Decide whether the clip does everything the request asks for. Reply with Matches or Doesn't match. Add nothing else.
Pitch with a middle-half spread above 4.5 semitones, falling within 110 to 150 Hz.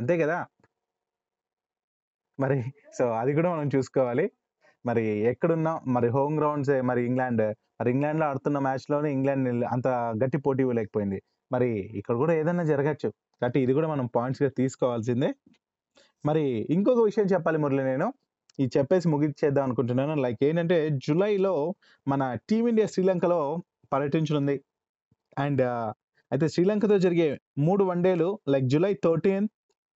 Matches